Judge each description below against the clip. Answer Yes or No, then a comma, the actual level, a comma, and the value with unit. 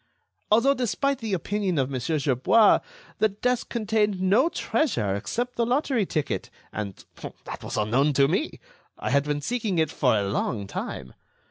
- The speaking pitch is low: No, high, 190 Hz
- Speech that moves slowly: No, average, 150 wpm